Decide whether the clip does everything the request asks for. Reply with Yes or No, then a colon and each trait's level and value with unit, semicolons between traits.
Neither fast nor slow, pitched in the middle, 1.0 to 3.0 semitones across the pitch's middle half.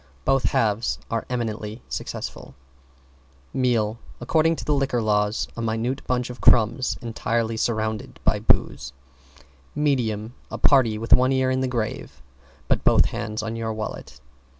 No: average, 145 wpm; low, 115 Hz; average, 2.7 semitones